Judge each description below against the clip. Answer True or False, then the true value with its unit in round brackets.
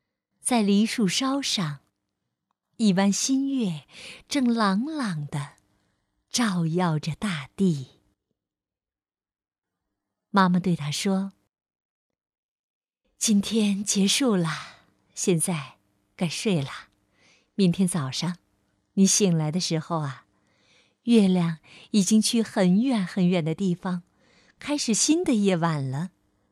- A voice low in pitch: False (185 Hz)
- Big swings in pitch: True (6.0 semitones)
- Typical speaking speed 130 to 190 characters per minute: True (145 characters per minute)